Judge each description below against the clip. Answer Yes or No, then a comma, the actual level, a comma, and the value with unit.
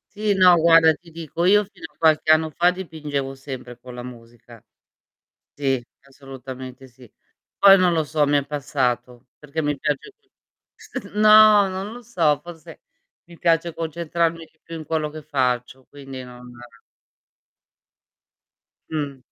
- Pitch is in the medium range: Yes, medium, 155 Hz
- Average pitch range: Yes, average, 4.2 semitones